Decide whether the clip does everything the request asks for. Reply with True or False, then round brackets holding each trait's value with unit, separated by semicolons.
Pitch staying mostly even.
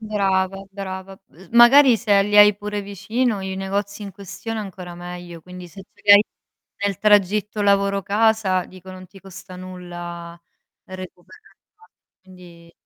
True (2.2 semitones)